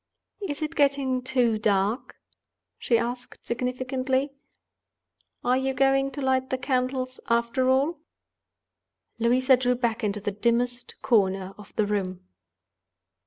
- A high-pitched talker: Yes, very high, 250 Hz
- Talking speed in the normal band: No, slow, 120 wpm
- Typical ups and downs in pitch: No, narrow, 2.2 semitones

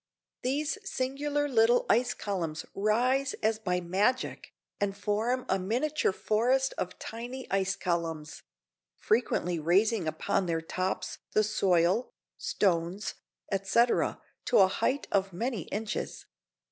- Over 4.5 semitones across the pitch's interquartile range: Yes, average, 5.2 semitones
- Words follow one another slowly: Yes, slow, 120 wpm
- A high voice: Yes, high, 210 Hz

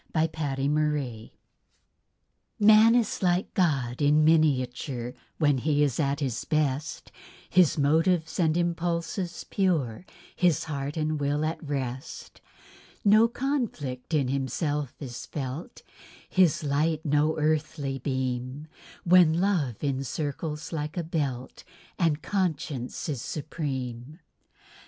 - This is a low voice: No, medium, 150 Hz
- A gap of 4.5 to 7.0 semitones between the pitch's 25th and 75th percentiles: No, average, 3.4 semitones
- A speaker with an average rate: No, slow, 115 wpm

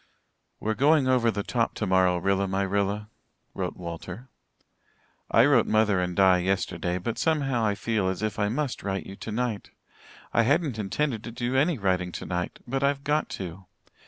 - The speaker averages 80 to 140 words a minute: No, average, 170 wpm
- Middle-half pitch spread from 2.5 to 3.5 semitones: No, average, 4.8 semitones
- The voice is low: Yes, low, 105 Hz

